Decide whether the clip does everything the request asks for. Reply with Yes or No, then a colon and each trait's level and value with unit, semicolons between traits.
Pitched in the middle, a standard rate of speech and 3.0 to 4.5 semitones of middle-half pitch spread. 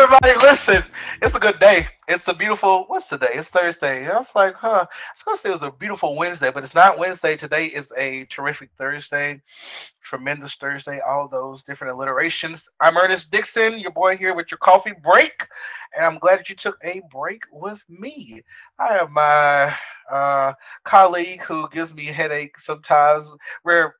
No: medium, 170 Hz; average, 185 wpm; average, 5.0 semitones